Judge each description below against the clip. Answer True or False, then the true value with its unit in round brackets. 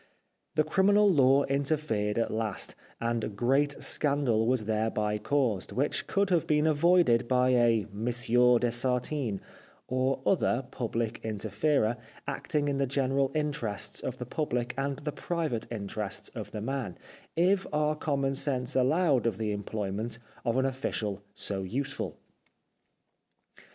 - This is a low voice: True (125 Hz)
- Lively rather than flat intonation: False (4.4 semitones)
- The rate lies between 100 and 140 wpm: True (135 wpm)